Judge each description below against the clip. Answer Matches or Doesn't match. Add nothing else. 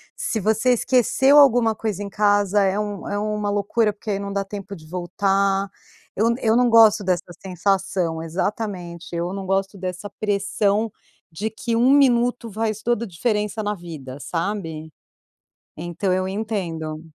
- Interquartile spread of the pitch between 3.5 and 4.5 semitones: Doesn't match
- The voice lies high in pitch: Matches